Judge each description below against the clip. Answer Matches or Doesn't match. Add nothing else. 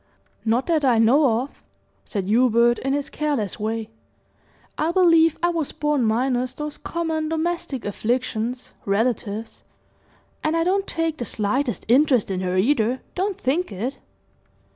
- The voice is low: Doesn't match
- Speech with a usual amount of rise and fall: Doesn't match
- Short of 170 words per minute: Matches